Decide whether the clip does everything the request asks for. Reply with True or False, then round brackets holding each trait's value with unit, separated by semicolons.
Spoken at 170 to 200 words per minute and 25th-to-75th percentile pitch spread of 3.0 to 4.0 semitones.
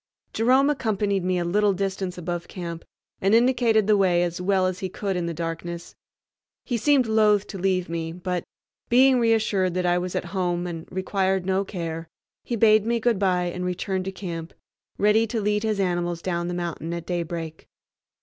True (190 wpm; 3.3 semitones)